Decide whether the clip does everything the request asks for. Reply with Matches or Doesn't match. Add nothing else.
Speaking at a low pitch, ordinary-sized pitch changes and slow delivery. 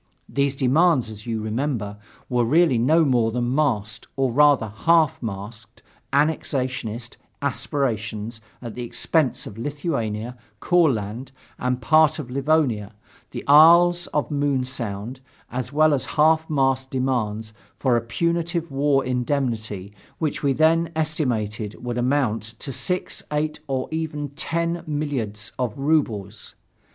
Matches